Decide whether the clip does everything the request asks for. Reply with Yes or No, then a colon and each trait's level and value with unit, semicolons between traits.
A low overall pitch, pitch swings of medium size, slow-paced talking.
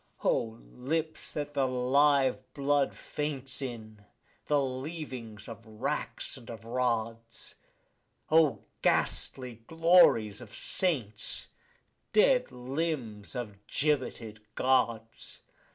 Yes: low, 130 Hz; average, 4.4 semitones; slow, 90 wpm